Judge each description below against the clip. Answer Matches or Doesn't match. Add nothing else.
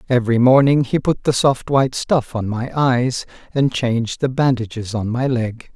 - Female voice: Doesn't match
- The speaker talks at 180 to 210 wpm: Matches